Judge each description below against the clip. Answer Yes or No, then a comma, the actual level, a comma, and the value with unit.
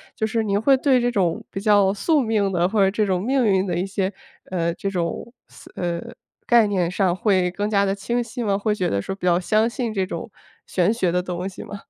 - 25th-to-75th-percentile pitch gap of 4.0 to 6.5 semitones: No, average, 3.2 semitones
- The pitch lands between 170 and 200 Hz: Yes, high, 195 Hz